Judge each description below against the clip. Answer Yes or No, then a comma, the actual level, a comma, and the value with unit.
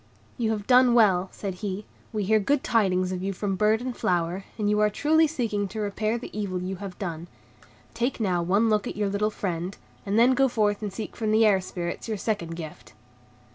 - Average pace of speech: No, fast, 215 wpm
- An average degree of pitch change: Yes, average, 3.1 semitones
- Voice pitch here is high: Yes, high, 205 Hz